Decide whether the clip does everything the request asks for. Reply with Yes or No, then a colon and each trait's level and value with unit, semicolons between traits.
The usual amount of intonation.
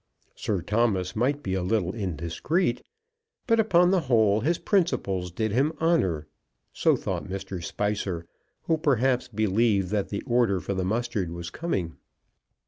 No: wide, 6.0 semitones